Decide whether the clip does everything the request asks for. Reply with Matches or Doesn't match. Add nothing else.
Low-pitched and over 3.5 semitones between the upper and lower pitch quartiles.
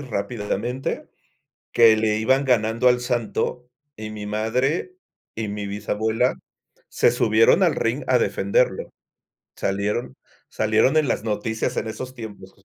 Doesn't match